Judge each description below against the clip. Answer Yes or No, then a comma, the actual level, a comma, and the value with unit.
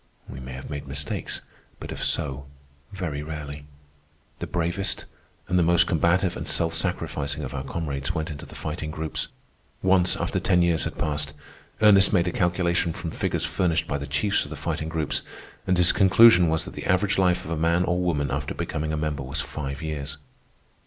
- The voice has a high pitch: No, very low, 80 Hz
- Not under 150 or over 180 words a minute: No, average, 195 wpm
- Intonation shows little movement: No, average, 3.5 semitones